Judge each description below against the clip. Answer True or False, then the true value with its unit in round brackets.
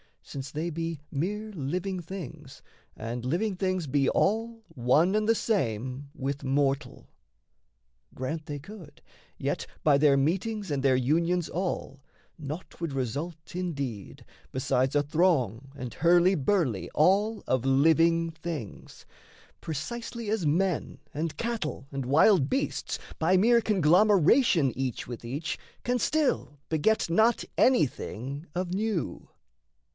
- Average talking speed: False (125 wpm)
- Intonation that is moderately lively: False (5.8 semitones)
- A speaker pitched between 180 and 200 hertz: False (160 Hz)